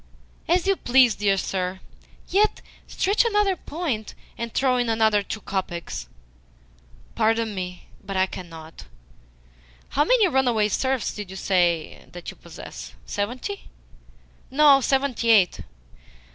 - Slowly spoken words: Yes, slow, 125 wpm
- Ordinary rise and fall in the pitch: No, wide, 6.3 semitones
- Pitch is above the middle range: Yes, high, 225 Hz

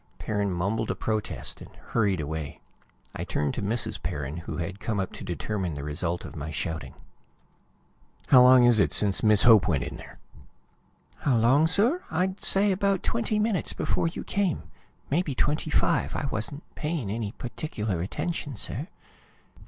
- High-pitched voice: No, low, 110 Hz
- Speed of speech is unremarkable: Yes, average, 165 wpm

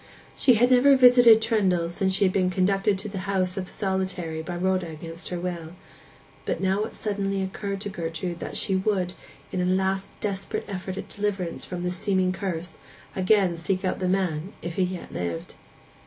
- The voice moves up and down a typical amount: No, narrow, 1.8 semitones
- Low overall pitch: No, high, 190 Hz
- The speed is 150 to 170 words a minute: No, average, 190 wpm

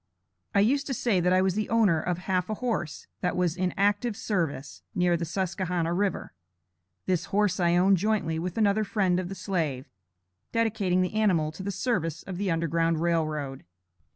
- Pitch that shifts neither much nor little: Yes, average, 3.3 semitones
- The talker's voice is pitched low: No, medium, 185 Hz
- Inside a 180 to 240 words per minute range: Yes, average, 185 wpm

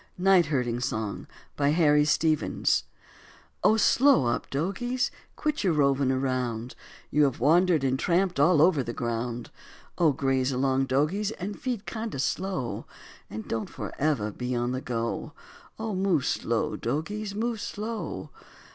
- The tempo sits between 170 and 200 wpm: No, average, 140 wpm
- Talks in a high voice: No, medium, 150 Hz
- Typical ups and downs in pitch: No, wide, 6.9 semitones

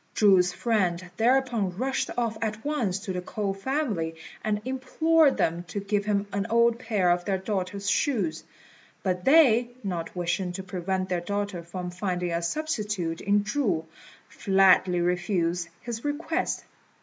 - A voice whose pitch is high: Yes, high, 200 Hz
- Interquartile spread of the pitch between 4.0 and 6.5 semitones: Yes, average, 4.5 semitones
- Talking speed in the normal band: Yes, average, 150 wpm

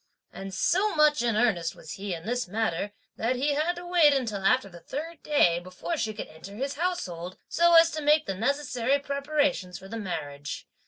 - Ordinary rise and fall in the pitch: No, wide, 7.7 semitones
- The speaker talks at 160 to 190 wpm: No, average, 200 wpm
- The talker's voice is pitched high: Yes, high, 245 Hz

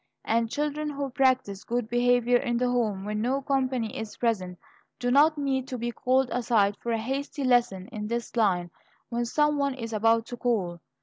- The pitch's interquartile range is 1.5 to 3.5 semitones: Yes, average, 2.9 semitones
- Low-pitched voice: No, high, 240 Hz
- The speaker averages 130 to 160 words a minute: No, average, 190 wpm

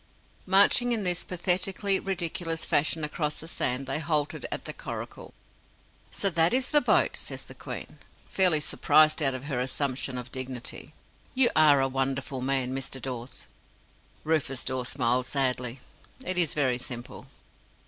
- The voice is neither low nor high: Yes, medium, 145 Hz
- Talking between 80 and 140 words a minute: No, average, 150 wpm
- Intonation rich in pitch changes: No, average, 4.7 semitones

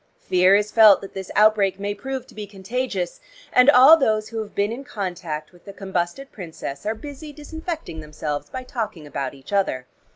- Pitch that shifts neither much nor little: No, wide, 5.8 semitones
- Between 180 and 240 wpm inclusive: Yes, average, 190 wpm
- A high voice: Yes, high, 205 Hz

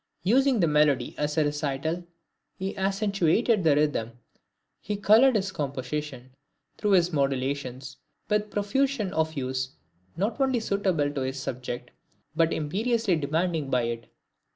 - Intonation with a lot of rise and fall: Yes, wide, 6.6 semitones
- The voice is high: No, medium, 160 Hz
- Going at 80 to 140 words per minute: Yes, slow, 135 wpm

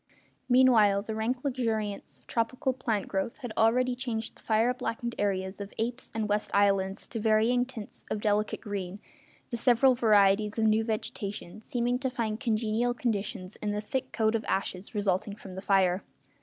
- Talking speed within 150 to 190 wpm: Yes, average, 170 wpm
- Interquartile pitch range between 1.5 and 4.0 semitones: Yes, average, 2.9 semitones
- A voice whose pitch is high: Yes, high, 220 Hz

